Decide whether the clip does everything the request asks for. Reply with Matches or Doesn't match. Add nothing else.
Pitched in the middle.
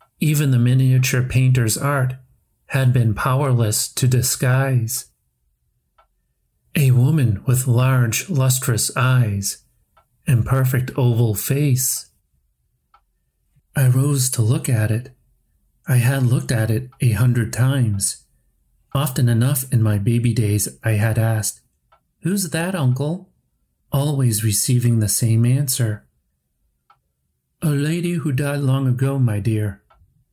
Doesn't match